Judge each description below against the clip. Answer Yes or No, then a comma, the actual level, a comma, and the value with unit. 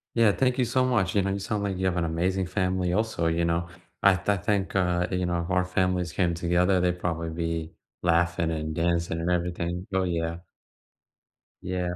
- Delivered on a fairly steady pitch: Yes, narrow, 1.9 semitones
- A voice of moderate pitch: No, very low, 90 Hz